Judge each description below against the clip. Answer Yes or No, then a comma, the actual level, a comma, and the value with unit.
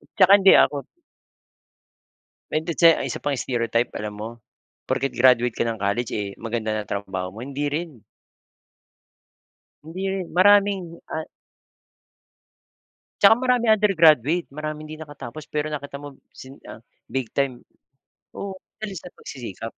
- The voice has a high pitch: No, medium, 145 Hz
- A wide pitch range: Yes, wide, 6.4 semitones